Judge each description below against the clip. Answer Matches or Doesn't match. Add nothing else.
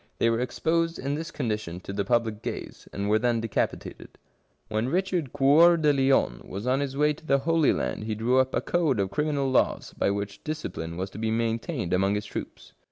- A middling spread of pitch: Doesn't match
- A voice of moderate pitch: Doesn't match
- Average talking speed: Doesn't match